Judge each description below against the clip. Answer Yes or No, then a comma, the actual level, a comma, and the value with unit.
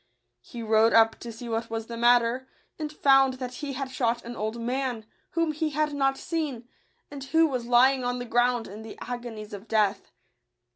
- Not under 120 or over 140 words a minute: No, average, 195 wpm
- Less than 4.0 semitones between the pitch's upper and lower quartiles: Yes, average, 3.0 semitones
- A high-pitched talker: Yes, high, 245 Hz